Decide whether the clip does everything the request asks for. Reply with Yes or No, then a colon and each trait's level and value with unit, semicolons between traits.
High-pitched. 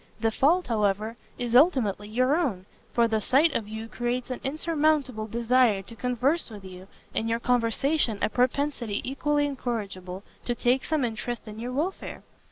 Yes: high, 240 Hz